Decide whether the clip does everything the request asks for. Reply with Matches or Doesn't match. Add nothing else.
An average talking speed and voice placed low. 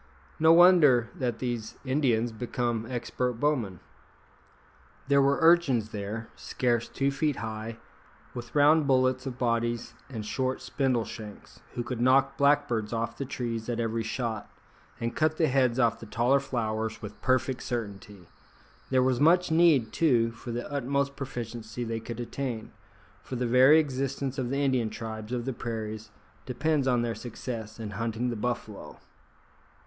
Matches